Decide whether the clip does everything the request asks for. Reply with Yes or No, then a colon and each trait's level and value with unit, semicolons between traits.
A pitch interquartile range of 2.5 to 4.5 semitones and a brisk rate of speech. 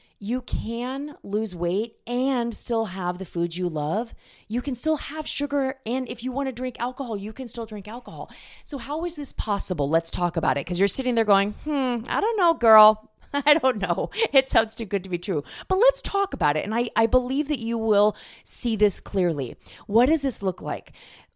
No: average, 5.1 semitones; fast, 215 wpm